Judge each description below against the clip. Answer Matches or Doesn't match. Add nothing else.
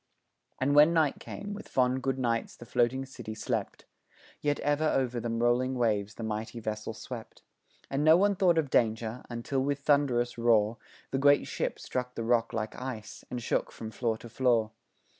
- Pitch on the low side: Matches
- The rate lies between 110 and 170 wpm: Doesn't match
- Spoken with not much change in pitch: Doesn't match